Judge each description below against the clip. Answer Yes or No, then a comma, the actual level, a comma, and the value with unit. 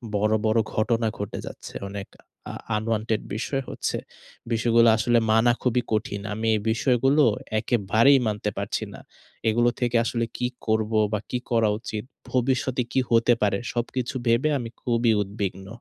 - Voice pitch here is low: Yes, low, 115 Hz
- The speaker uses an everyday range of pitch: No, narrow, 2.1 semitones